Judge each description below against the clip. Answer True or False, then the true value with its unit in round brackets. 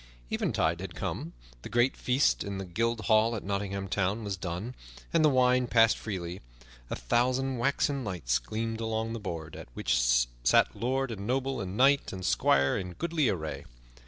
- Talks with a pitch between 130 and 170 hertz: False (110 Hz)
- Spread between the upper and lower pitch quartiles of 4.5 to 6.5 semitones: True (5.3 semitones)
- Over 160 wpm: True (175 wpm)